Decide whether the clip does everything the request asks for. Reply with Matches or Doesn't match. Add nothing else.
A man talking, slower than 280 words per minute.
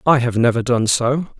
Matches